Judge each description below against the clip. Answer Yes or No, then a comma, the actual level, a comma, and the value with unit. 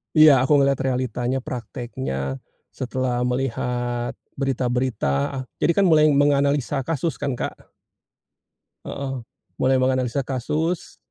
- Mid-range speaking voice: No, low, 130 Hz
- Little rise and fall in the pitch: Yes, narrow, 2.3 semitones